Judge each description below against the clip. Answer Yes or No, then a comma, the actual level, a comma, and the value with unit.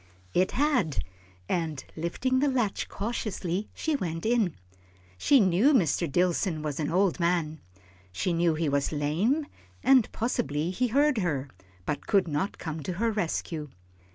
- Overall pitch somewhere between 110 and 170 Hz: No, medium, 180 Hz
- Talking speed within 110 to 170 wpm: Yes, average, 150 wpm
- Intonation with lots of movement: Yes, wide, 6.6 semitones